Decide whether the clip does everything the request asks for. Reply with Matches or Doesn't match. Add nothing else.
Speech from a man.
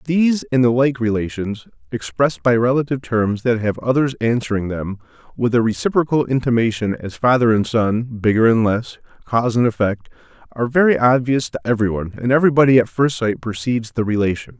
Matches